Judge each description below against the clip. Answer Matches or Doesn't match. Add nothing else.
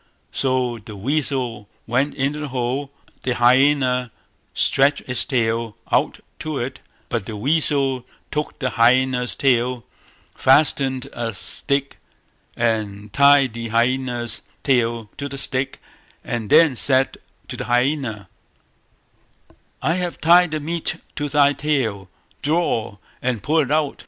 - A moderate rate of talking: Doesn't match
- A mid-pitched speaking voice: Doesn't match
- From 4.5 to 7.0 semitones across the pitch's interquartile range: Doesn't match